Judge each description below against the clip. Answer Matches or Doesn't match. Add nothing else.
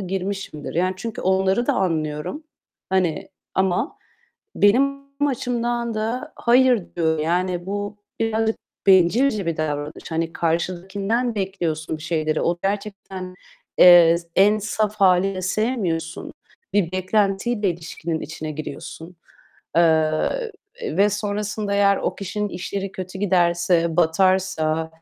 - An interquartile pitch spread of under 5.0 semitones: Matches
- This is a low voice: Doesn't match